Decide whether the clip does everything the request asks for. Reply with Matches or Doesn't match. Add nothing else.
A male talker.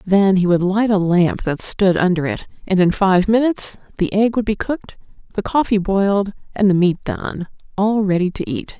Doesn't match